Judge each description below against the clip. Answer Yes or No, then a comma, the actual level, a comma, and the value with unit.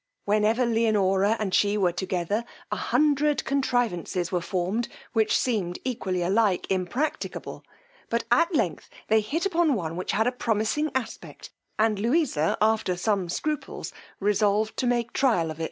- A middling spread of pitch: Yes, average, 4.7 semitones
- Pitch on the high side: Yes, high, 215 Hz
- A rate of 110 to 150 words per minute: Yes, average, 145 wpm